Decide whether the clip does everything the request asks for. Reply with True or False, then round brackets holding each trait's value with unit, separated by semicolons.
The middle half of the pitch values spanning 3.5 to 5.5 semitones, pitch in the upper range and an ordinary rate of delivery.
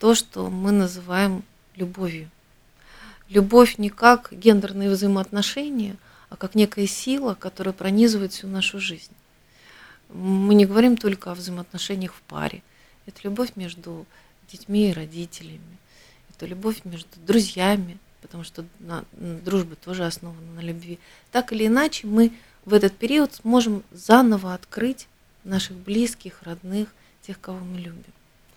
False (3.1 semitones; 195 Hz; 130 wpm)